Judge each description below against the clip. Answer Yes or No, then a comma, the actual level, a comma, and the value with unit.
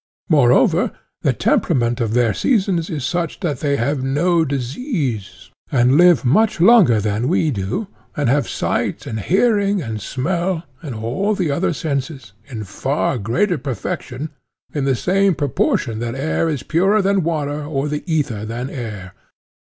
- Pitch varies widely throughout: Yes, wide, 6.2 semitones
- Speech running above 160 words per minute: No, average, 155 wpm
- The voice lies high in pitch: No, medium, 145 Hz